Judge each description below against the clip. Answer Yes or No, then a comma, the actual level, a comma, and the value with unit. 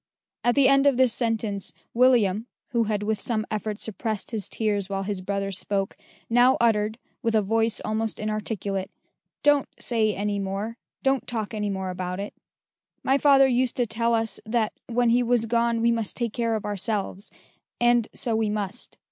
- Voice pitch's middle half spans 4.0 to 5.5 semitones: No, narrow, 2.5 semitones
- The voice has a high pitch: Yes, high, 220 Hz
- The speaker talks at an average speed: Yes, average, 180 wpm